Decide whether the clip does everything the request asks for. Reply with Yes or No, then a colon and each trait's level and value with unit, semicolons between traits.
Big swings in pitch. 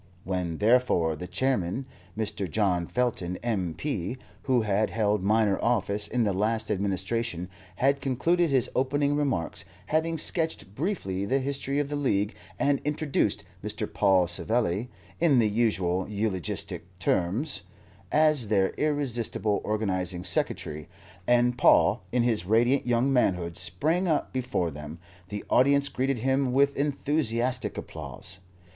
Yes: wide, 6.2 semitones